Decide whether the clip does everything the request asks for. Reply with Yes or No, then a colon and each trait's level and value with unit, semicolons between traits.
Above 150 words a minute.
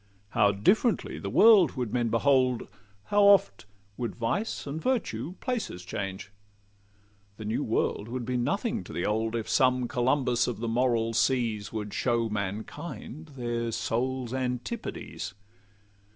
No: slow, 135 wpm